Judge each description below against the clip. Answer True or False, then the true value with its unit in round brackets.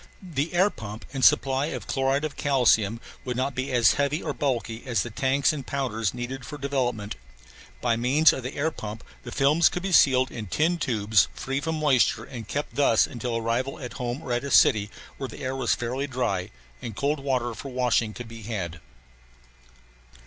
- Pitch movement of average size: True (3.4 semitones)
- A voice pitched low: True (130 Hz)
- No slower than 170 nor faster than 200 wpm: True (195 wpm)